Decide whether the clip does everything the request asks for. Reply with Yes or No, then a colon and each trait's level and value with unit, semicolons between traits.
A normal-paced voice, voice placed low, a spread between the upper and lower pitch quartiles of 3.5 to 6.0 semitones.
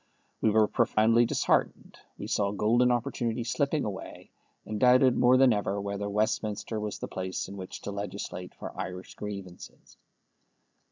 No: average, 150 wpm; low, 105 Hz; average, 3.0 semitones